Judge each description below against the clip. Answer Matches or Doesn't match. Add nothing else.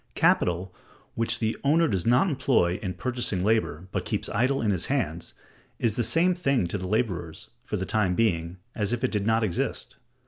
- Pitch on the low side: Matches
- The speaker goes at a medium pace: Matches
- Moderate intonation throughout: Matches